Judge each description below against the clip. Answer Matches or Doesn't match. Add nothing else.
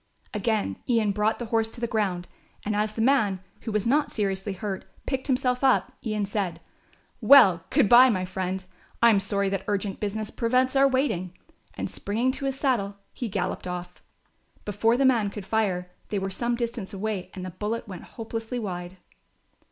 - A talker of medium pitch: Doesn't match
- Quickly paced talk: Doesn't match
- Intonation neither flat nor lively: Matches